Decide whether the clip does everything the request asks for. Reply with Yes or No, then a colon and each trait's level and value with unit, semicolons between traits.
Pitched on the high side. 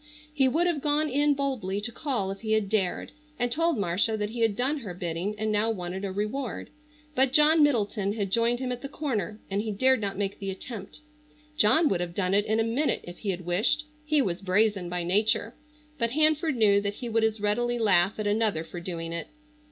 Yes: high, 215 Hz